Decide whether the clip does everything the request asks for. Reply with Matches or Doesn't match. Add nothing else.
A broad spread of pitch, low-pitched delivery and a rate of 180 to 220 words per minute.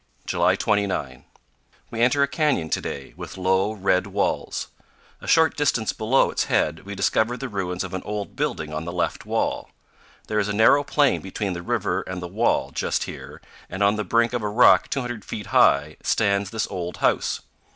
Doesn't match